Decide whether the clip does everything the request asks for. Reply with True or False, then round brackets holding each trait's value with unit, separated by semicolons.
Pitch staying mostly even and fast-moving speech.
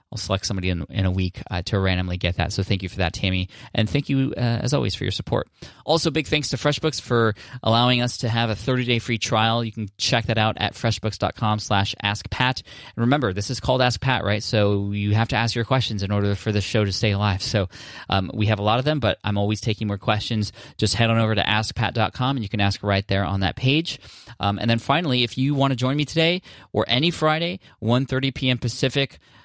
False (3.9 semitones; 245 wpm)